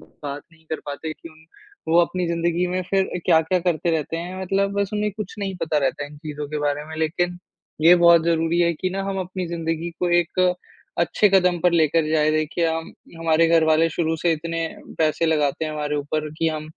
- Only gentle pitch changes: Yes, narrow, 2.2 semitones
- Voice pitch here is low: No, medium, 165 Hz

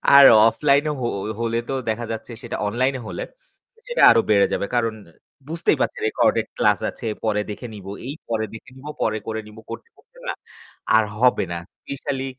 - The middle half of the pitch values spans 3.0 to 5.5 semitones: Yes, average, 3.6 semitones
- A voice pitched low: Yes, low, 115 Hz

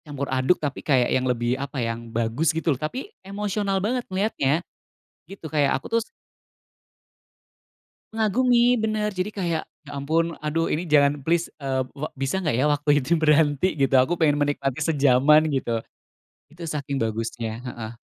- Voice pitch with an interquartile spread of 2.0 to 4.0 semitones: No, average, 5.2 semitones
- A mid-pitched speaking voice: Yes, medium, 150 Hz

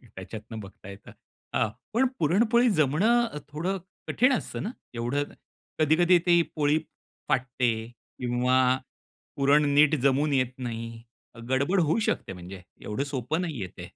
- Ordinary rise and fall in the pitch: No, wide, 6.5 semitones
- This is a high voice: No, medium, 140 Hz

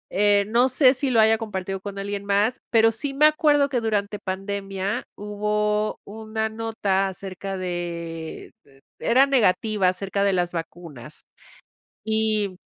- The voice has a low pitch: No, high, 205 Hz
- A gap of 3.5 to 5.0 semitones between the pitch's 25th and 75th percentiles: No, average, 2.7 semitones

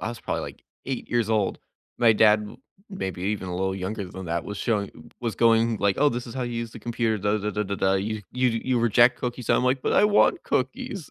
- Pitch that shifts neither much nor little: Yes, average, 3.2 semitones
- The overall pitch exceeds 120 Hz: No, low, 115 Hz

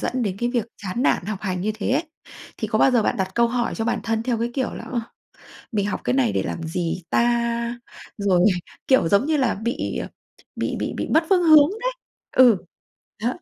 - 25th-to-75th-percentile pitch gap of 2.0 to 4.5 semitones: Yes, average, 4.0 semitones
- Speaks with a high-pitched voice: Yes, high, 235 Hz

